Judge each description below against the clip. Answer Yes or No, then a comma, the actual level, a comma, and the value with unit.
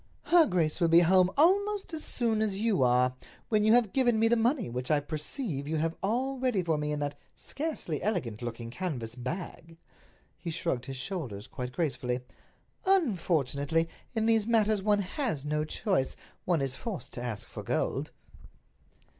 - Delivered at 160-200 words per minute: Yes, average, 165 wpm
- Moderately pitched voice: Yes, medium, 175 Hz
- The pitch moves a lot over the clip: Yes, wide, 8.1 semitones